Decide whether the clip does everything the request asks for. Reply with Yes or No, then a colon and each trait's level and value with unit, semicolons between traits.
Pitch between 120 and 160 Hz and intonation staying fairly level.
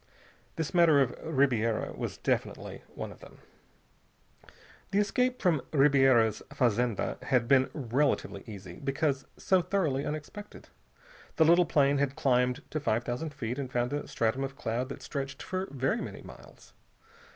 No: low, 135 Hz; average, 3.9 semitones